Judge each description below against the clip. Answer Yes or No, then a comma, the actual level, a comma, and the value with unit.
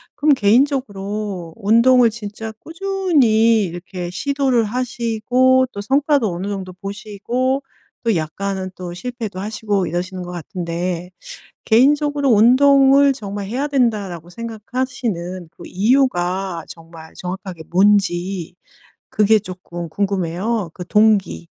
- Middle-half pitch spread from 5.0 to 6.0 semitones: Yes, wide, 5.5 semitones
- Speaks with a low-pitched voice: No, high, 205 Hz